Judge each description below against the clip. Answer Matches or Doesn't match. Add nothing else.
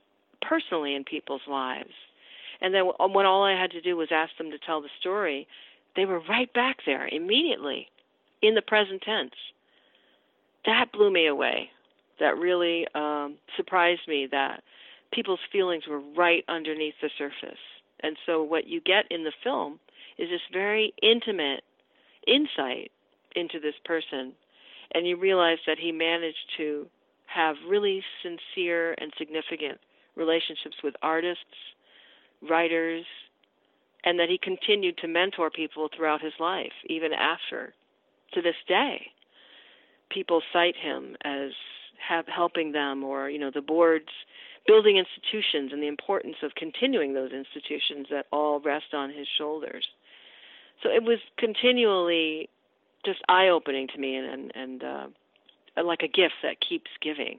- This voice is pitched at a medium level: Matches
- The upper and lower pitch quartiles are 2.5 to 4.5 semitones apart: Matches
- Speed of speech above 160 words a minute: Doesn't match